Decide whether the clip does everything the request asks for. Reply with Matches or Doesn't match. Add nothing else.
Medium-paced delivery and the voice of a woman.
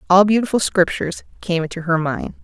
Matches